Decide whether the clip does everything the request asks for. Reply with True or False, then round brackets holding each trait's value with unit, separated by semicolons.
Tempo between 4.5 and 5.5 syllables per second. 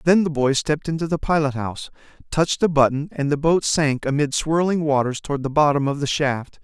False (5.8 syllables/s)